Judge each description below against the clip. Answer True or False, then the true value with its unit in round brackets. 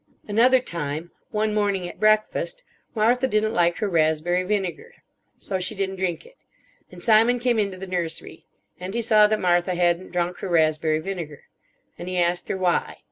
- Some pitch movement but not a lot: True (3.6 semitones)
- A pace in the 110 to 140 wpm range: False (175 wpm)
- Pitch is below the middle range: False (185 Hz)